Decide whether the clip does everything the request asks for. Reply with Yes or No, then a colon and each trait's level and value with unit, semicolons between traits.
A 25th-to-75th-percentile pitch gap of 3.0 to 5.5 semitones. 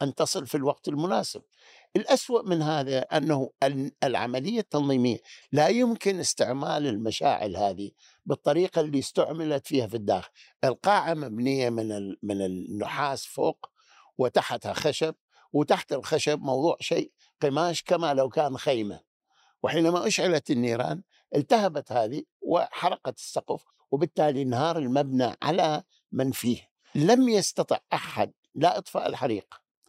Yes: average, 4.3 semitones